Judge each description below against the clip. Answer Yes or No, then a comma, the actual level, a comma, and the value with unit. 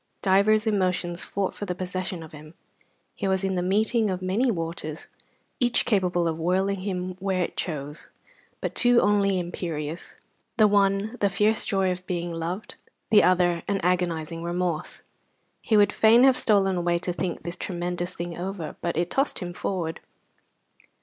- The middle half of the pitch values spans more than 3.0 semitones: No, narrow, 2.6 semitones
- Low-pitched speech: No, medium, 185 Hz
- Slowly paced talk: No, average, 165 wpm